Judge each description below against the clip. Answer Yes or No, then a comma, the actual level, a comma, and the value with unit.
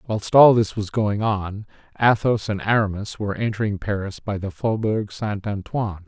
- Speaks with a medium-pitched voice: No, low, 105 Hz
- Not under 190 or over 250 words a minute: No, average, 170 wpm